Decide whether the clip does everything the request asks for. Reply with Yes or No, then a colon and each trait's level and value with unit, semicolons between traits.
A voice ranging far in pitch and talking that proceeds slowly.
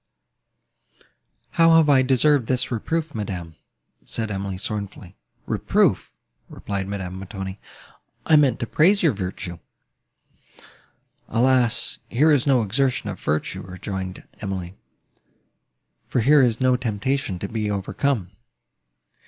Yes: wide, 5.7 semitones; slow, 115 wpm